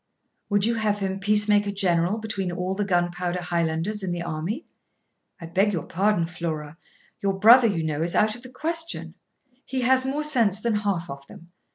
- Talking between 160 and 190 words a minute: Yes, average, 185 wpm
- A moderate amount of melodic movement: Yes, average, 3.9 semitones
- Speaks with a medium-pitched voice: No, high, 195 Hz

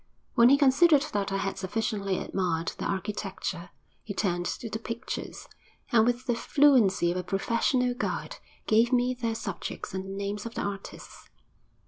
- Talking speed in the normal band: Yes, average, 165 wpm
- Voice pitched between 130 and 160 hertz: No, high, 215 Hz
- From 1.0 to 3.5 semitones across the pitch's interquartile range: No, average, 4.0 semitones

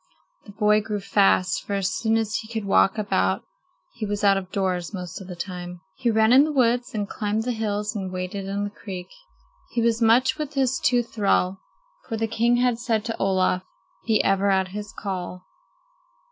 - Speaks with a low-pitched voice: No, high, 210 Hz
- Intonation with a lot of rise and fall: No, average, 2.8 semitones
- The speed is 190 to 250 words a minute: Yes, average, 200 wpm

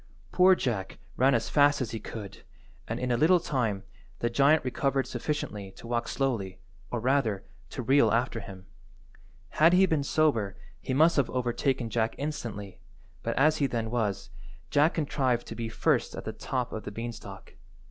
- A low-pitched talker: Yes, low, 125 Hz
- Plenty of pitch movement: No, average, 4.2 semitones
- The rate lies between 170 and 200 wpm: Yes, average, 175 wpm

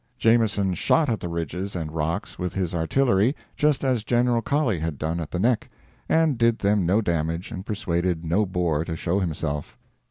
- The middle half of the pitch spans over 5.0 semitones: Yes, wide, 5.4 semitones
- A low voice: Yes, very low, 95 Hz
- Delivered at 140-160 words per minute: No, average, 185 wpm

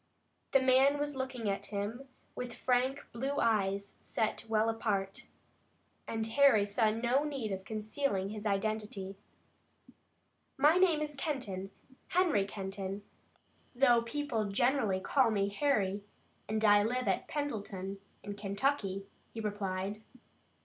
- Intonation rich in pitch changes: No, average, 5.0 semitones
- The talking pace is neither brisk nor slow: No, slow, 125 wpm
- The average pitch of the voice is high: Yes, high, 220 Hz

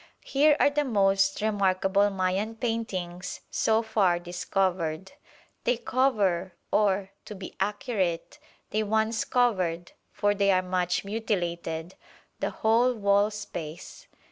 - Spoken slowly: Yes, slow, 115 wpm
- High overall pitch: Yes, high, 200 Hz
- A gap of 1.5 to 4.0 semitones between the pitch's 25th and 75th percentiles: Yes, average, 3.2 semitones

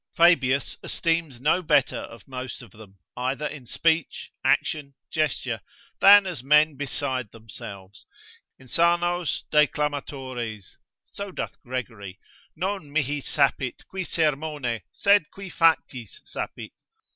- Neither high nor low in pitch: Yes, medium, 145 Hz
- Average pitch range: Yes, average, 4.6 semitones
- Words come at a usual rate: No, slow, 110 wpm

